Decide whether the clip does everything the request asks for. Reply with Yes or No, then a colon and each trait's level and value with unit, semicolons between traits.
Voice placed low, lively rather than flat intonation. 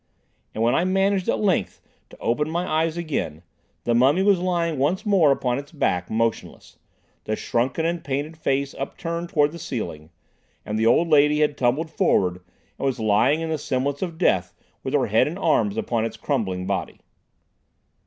No: medium, 145 Hz; wide, 6.2 semitones